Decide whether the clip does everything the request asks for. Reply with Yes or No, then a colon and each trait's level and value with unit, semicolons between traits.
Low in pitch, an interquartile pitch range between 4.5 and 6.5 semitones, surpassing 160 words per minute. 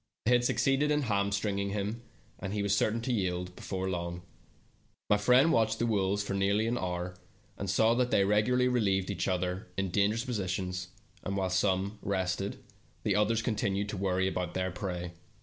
No: low, 100 Hz; average, 3.0 semitones; average, 175 wpm